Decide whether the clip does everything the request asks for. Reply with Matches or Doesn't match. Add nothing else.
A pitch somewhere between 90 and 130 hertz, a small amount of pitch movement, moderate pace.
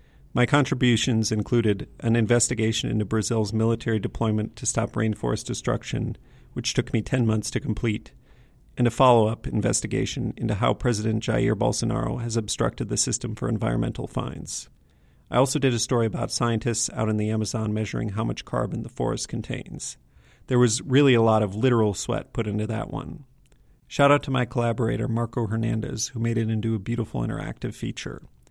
Matches